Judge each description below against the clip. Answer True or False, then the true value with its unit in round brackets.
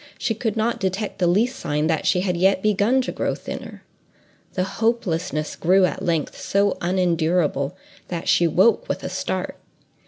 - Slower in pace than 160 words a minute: False (165 wpm)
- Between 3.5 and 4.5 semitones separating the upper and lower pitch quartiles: True (3.8 semitones)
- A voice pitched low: False (185 Hz)